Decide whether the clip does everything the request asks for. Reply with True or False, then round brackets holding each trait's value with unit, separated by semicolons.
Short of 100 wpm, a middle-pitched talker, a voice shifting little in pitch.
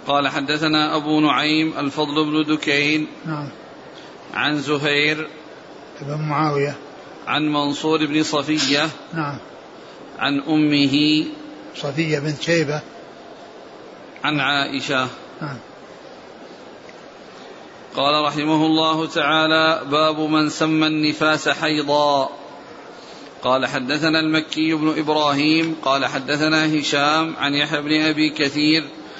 True (90 wpm; 150 Hz; 1.3 semitones)